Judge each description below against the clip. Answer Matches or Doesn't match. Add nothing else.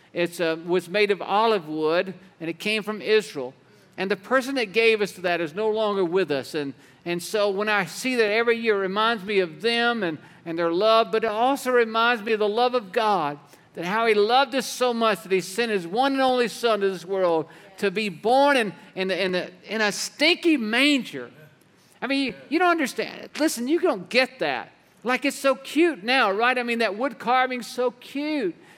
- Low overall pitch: Doesn't match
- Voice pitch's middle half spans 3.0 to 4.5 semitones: Doesn't match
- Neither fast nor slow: Doesn't match